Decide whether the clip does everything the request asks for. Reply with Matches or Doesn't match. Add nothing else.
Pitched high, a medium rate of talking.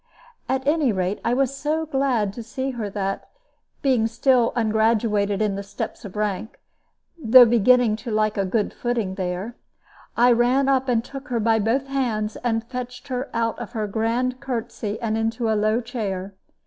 Matches